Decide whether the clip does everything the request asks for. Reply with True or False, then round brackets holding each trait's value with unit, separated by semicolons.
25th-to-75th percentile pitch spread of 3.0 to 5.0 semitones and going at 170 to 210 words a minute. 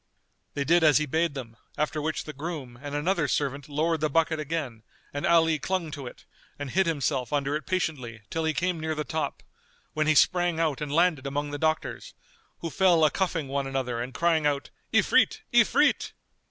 False (2.6 semitones; 195 wpm)